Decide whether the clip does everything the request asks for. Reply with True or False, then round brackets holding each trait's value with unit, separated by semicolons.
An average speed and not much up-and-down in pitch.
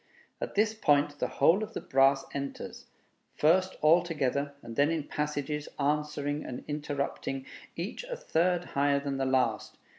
False (155 wpm; 3.0 semitones)